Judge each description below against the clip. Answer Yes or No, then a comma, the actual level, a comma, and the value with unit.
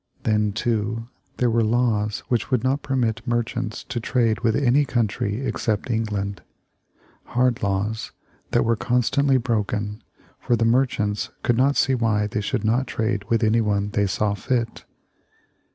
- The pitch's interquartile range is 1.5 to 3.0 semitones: Yes, narrow, 2.6 semitones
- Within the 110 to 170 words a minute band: Yes, average, 150 wpm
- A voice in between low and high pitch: No, low, 115 Hz